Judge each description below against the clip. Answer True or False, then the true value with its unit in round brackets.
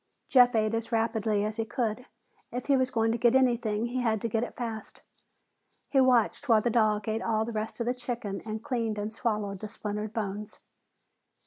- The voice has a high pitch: True (225 Hz)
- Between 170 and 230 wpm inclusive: True (205 wpm)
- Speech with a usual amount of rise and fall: False (2.1 semitones)